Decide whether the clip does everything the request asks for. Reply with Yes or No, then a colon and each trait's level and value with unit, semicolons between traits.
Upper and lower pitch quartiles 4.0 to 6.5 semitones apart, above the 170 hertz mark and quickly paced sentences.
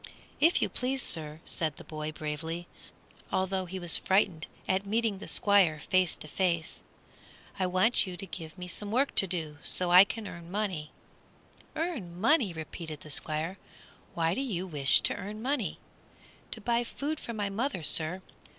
No: average, 4.5 semitones; medium, 185 Hz; average, 175 wpm